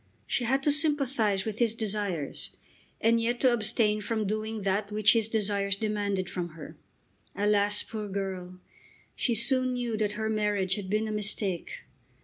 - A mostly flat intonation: Yes, narrow, 2.2 semitones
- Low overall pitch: No, high, 210 Hz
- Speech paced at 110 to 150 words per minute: No, average, 160 wpm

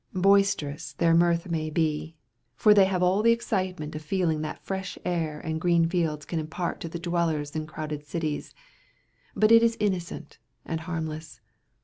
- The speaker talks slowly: No, average, 165 wpm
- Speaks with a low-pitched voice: No, medium, 165 Hz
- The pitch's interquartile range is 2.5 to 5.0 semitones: Yes, average, 2.9 semitones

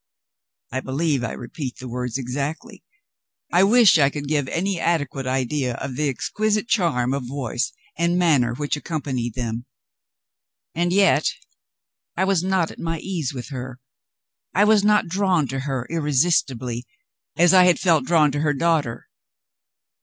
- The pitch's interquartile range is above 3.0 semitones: Yes, average, 5.2 semitones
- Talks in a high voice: No, medium, 145 Hz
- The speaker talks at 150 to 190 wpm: Yes, average, 155 wpm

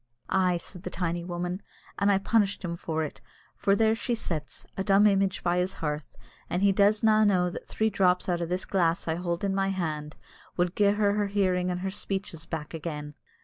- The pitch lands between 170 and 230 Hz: Yes, medium, 185 Hz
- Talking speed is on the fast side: Yes, fast, 215 wpm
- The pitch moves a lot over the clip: No, average, 2.7 semitones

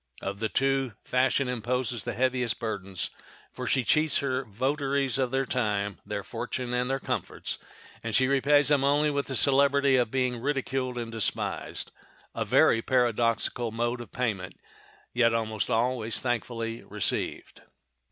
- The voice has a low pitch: Yes, low, 125 Hz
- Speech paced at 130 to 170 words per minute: Yes, average, 145 wpm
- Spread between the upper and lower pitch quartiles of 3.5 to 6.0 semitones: No, average, 2.9 semitones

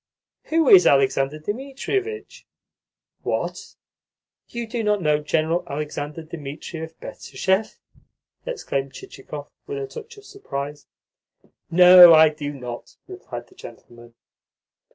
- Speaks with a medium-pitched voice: Yes, medium, 160 Hz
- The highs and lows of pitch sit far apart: Yes, wide, 8.6 semitones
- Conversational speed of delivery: No, slow, 110 wpm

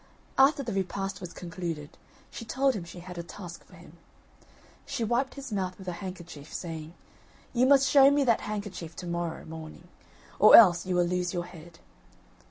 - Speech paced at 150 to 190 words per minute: Yes, average, 180 wpm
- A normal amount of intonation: Yes, average, 4.5 semitones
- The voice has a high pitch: No, medium, 180 Hz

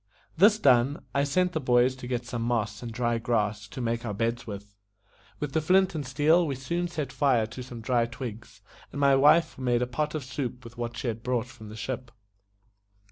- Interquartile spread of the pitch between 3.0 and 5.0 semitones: Yes, average, 3.4 semitones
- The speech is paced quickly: Yes, fast, 215 wpm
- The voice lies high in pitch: No, low, 125 Hz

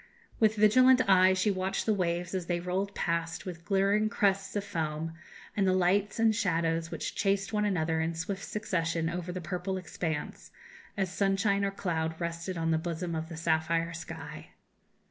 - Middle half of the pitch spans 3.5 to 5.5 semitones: No, average, 3.0 semitones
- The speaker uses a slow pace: No, average, 175 wpm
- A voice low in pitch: No, medium, 180 Hz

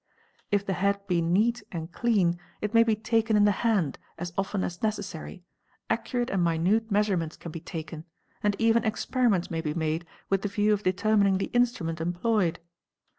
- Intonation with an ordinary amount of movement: Yes, average, 4.2 semitones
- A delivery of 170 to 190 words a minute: Yes, average, 180 wpm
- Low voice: No, high, 200 Hz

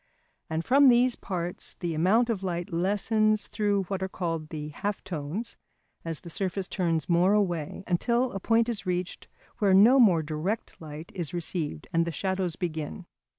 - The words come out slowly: No, average, 170 wpm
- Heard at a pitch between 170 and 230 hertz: Yes, medium, 185 Hz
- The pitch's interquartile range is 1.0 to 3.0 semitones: No, average, 3.9 semitones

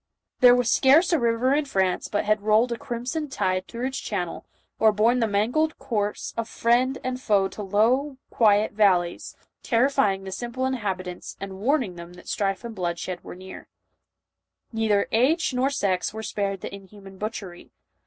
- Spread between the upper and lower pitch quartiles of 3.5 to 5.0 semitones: Yes, average, 4.4 semitones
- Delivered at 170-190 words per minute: Yes, average, 175 wpm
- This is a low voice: No, high, 220 Hz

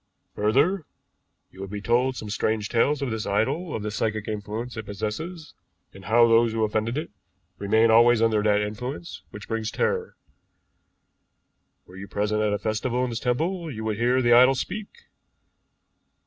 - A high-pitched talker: No, low, 115 Hz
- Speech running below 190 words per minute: Yes, average, 170 wpm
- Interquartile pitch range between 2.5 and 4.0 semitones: Yes, average, 3.1 semitones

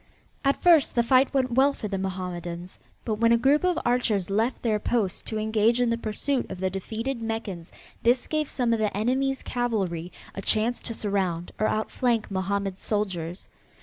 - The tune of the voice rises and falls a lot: No, average, 4.1 semitones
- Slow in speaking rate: No, average, 180 wpm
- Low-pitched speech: No, high, 220 Hz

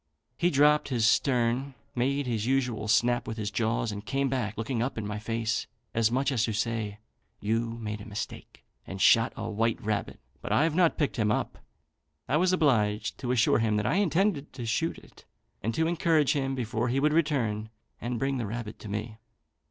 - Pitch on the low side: Yes, low, 120 Hz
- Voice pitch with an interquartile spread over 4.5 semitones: No, average, 4.0 semitones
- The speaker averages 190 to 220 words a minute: Yes, average, 200 wpm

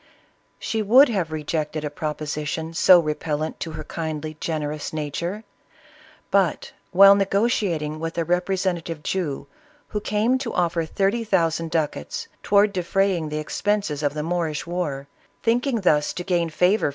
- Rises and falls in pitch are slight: No, average, 4.2 semitones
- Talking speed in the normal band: Yes, average, 160 wpm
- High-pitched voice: No, medium, 170 Hz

